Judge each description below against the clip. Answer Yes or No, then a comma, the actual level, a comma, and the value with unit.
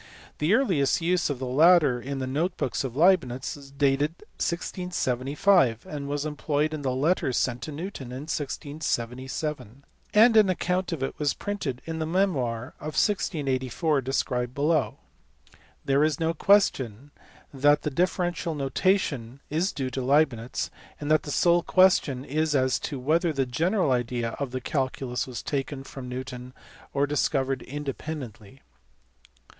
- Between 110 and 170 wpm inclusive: Yes, average, 150 wpm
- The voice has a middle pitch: Yes, medium, 145 Hz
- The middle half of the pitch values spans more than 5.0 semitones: No, average, 3.9 semitones